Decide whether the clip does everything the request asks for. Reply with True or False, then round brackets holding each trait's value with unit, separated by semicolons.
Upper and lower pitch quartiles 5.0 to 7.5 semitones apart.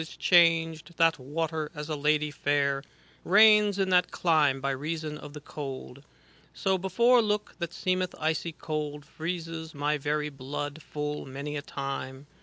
False (2.6 semitones)